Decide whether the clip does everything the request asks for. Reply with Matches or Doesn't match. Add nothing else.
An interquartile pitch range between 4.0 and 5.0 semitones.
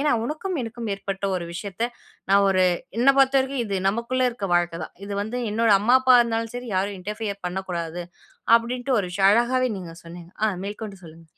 Matches